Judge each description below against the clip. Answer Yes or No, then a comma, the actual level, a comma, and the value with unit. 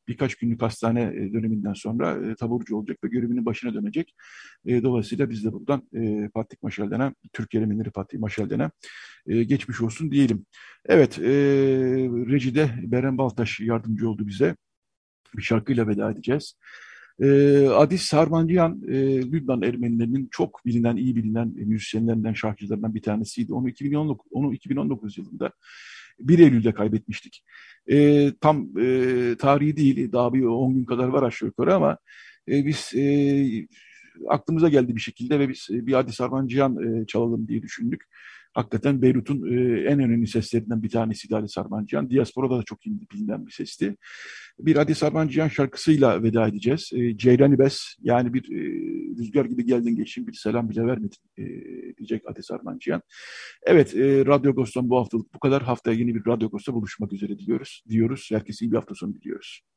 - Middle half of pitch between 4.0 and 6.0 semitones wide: No, average, 3.6 semitones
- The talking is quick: Yes, fast, 150 wpm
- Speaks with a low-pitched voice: Yes, low, 125 Hz